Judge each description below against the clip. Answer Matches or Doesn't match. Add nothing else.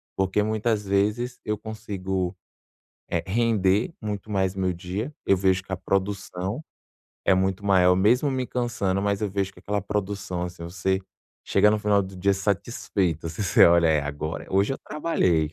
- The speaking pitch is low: Matches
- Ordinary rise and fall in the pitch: Doesn't match